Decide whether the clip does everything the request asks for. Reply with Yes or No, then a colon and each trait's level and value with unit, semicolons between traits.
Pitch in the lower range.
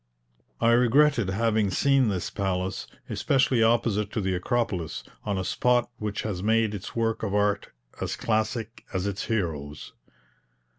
Yes: low, 110 Hz